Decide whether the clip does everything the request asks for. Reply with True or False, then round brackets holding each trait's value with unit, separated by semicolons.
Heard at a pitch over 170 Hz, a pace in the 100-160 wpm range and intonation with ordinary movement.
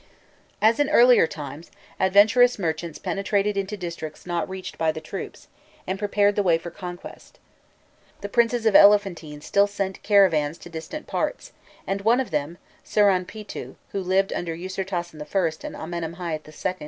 True (190 Hz; 155 wpm; 3.7 semitones)